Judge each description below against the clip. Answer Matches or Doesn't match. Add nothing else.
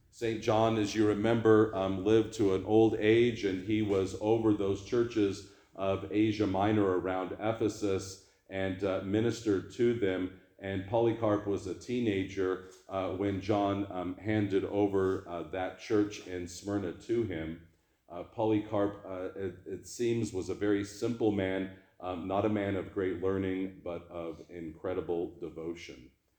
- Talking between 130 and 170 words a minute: Matches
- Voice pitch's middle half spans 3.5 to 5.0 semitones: Doesn't match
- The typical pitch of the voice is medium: Doesn't match